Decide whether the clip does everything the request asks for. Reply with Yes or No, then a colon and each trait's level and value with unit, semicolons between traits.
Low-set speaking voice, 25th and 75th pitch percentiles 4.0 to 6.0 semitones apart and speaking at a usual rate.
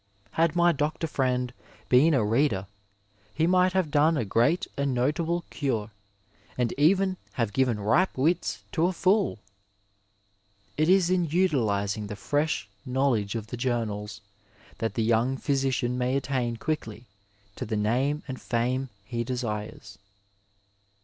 Yes: low, 130 Hz; wide, 5.6 semitones; average, 145 wpm